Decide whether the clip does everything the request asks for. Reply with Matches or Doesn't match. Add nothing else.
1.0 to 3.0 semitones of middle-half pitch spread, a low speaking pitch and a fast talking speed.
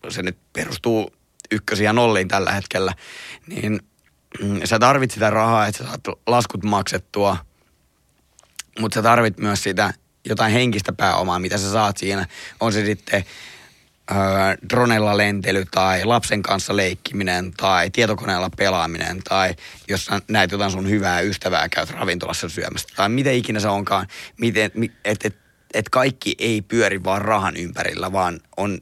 Doesn't match